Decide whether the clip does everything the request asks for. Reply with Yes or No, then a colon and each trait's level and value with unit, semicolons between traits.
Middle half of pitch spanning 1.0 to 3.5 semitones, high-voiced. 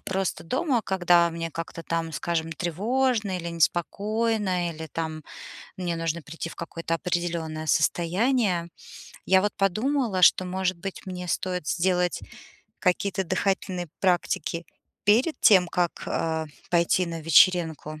No: narrow, 2.5 semitones; medium, 175 Hz